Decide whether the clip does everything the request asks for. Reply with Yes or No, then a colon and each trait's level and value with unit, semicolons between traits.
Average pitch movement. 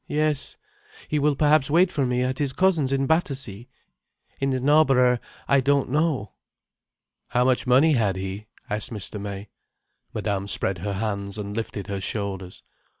No: wide, 5.9 semitones